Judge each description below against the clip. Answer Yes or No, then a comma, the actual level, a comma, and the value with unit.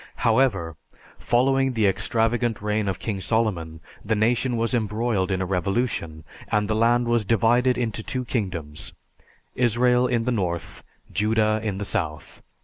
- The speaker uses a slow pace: No, average, 145 wpm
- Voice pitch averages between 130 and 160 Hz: No, low, 110 Hz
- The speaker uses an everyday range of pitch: Yes, average, 3.6 semitones